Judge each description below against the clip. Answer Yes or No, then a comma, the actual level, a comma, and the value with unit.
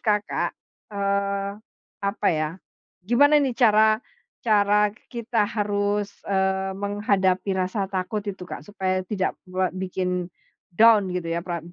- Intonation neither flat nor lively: No, narrow, 1.9 semitones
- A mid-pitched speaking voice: No, high, 200 Hz